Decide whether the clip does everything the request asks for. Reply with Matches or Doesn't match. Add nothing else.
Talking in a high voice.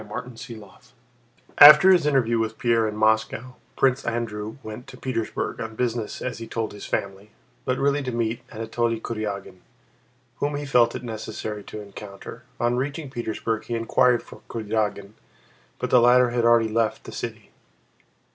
Doesn't match